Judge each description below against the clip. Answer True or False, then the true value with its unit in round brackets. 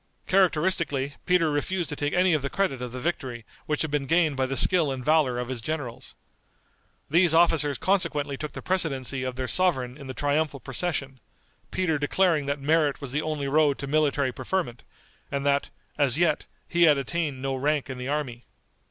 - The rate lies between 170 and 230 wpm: True (190 wpm)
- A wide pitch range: False (3.3 semitones)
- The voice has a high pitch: False (145 Hz)